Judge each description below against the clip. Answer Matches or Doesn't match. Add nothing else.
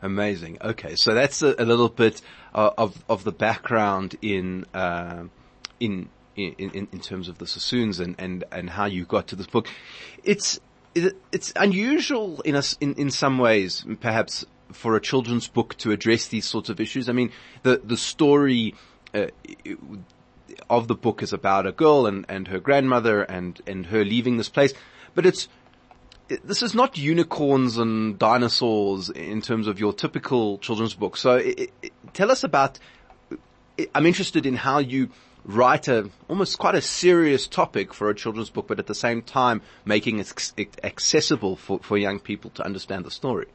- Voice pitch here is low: Matches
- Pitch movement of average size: Doesn't match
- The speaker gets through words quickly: Doesn't match